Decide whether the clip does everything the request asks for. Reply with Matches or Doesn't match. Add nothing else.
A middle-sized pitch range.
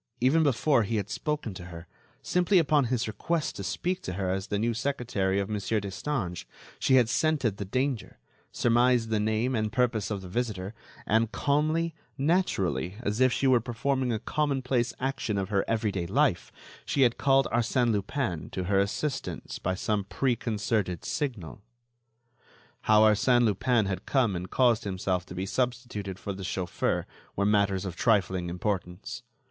Matches